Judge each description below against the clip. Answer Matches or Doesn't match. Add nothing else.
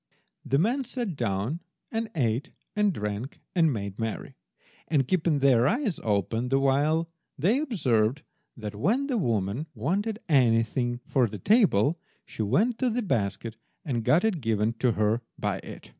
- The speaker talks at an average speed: Matches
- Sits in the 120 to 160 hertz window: Matches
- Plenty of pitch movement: Matches